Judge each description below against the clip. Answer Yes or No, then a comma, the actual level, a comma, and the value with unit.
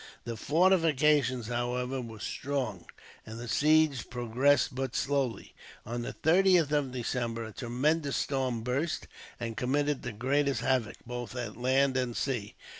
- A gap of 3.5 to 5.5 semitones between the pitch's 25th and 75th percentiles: No, average, 3.1 semitones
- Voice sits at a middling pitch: No, low, 130 Hz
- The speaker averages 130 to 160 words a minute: Yes, average, 140 wpm